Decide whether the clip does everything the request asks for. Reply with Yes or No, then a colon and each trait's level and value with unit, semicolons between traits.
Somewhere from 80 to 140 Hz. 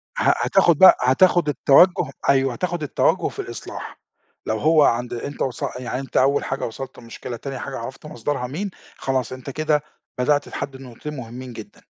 Yes: low, 135 Hz